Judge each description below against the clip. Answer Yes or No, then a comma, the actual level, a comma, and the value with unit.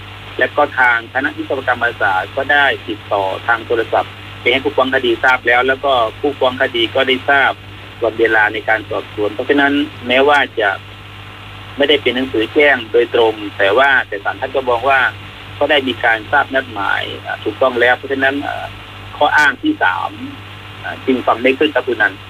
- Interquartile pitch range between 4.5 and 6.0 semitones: Yes, average, 4.9 semitones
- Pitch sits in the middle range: No, low, 125 Hz